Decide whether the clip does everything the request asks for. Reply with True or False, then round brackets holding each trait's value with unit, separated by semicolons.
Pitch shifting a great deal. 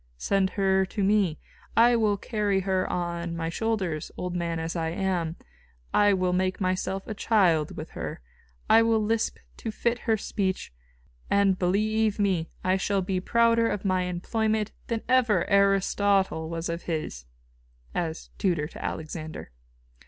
False (3.6 semitones)